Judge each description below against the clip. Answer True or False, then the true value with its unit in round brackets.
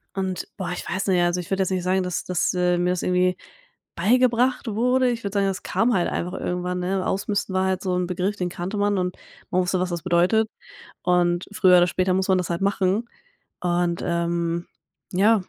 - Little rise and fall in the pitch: True (1.8 semitones)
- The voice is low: False (185 Hz)